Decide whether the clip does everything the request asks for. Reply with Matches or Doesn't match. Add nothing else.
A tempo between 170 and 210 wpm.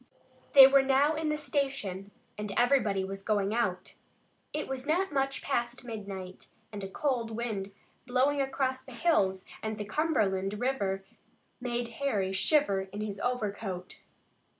Doesn't match